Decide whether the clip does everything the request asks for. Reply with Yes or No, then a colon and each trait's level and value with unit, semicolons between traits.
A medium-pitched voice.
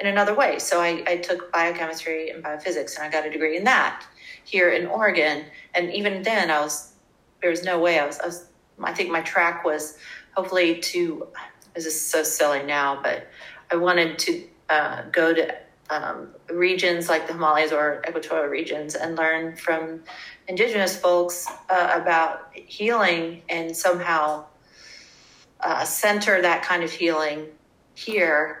Yes: medium, 165 Hz